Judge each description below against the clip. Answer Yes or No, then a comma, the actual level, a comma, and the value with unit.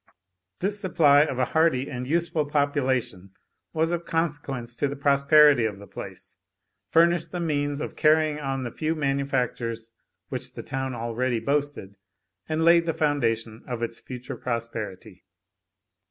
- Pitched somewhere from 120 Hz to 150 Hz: Yes, medium, 140 Hz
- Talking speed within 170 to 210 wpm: No, average, 145 wpm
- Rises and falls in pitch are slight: No, average, 4.4 semitones